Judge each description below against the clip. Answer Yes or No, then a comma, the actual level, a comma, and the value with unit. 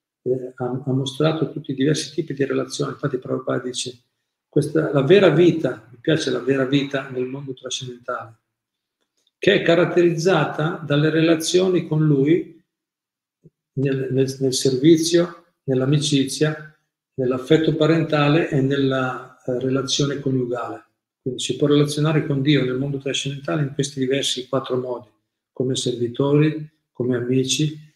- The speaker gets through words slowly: No, average, 135 wpm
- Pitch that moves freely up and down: No, average, 3.1 semitones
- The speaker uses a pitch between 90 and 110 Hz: No, medium, 140 Hz